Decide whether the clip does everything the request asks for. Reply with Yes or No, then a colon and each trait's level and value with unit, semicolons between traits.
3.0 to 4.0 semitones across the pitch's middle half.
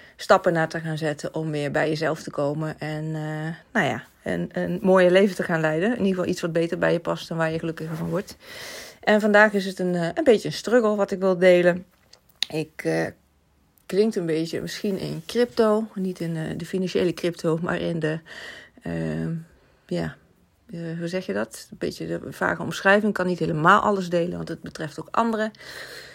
Yes: average, 3.6 semitones